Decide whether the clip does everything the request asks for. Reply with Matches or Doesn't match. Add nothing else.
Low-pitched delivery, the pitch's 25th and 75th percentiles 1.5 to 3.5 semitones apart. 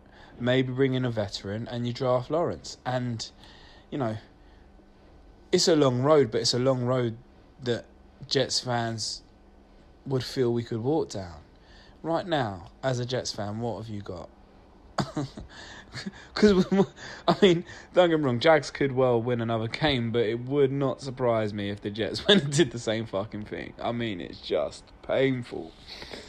Doesn't match